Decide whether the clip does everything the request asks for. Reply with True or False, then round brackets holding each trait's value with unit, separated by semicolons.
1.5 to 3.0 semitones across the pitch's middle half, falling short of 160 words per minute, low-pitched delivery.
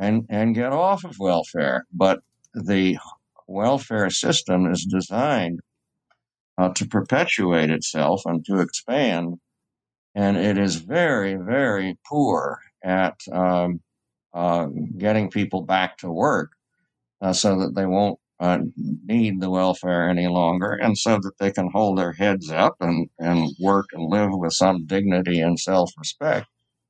True (2.6 semitones; 145 wpm; 95 Hz)